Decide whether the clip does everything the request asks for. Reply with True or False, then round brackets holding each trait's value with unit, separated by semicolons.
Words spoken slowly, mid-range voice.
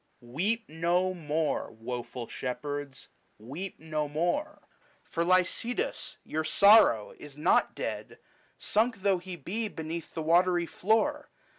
True (120 wpm; 170 Hz)